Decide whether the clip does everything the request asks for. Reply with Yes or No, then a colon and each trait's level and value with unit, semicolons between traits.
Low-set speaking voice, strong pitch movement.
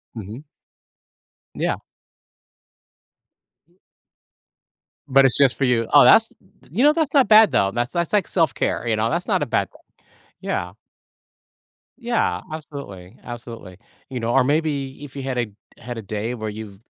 Yes: low, 130 Hz; wide, 6.1 semitones